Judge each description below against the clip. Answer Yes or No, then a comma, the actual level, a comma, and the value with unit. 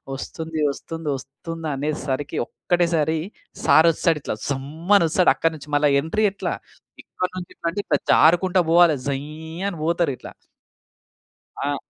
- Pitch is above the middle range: No, medium, 160 Hz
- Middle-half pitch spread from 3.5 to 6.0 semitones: No, average, 3.0 semitones